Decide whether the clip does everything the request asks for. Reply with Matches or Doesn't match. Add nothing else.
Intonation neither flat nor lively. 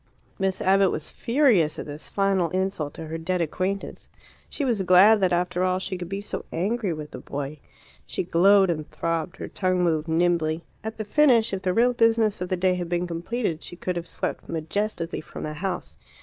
Matches